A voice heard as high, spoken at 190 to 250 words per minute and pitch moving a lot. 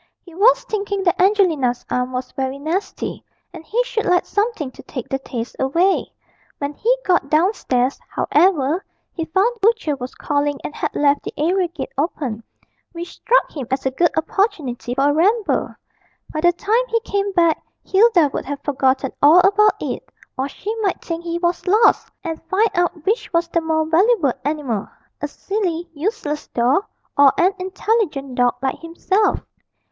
No: very high, 335 Hz; average, 175 wpm; wide, 5.7 semitones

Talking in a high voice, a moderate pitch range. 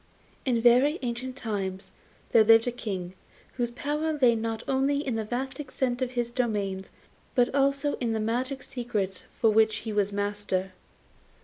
Yes: high, 235 Hz; average, 3.6 semitones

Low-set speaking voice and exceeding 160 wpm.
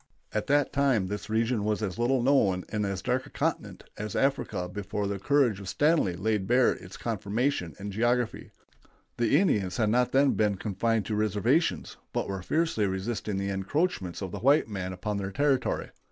Yes: low, 110 Hz; average, 180 wpm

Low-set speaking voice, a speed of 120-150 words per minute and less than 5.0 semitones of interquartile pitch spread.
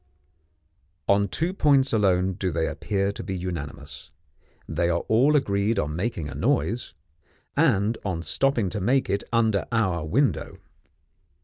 No: low, 100 Hz; average, 140 wpm; average, 5.3 semitones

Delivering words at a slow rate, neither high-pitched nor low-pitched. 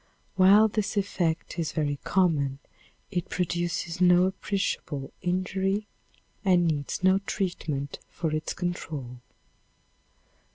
Yes: slow, 100 wpm; medium, 175 Hz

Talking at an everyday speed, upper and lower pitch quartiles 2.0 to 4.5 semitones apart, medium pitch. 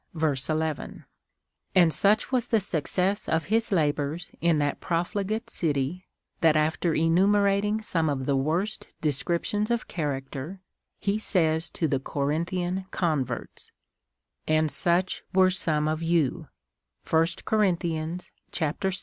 No: slow, 130 wpm; average, 3.7 semitones; medium, 165 Hz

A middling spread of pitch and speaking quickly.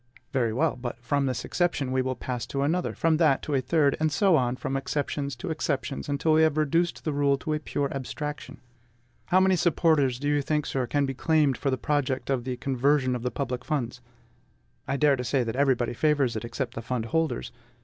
Yes: average, 3.1 semitones; fast, 220 wpm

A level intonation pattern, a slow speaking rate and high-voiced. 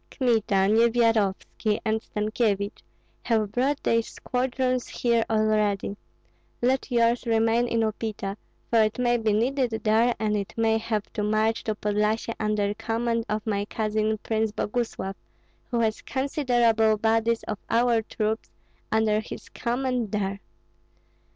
Yes: narrow, 1.8 semitones; slow, 130 wpm; high, 225 Hz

